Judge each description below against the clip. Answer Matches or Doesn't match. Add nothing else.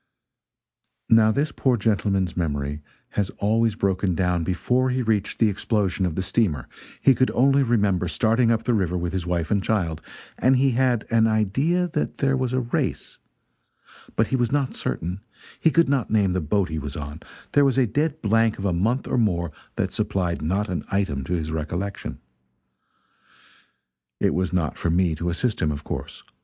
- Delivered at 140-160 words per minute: Doesn't match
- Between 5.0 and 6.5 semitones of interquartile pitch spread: Matches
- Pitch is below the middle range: Matches